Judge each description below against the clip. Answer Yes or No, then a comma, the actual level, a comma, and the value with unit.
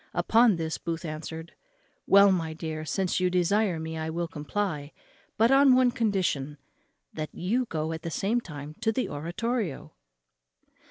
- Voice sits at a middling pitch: Yes, medium, 170 Hz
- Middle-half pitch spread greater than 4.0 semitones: Yes, average, 5.0 semitones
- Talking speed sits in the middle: Yes, average, 155 wpm